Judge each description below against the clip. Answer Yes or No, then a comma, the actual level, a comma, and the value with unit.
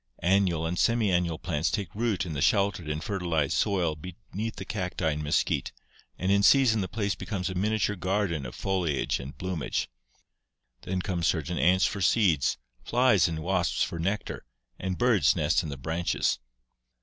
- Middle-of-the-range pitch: No, very low, 90 Hz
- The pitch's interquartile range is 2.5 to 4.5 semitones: Yes, average, 3.6 semitones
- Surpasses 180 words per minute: No, average, 165 wpm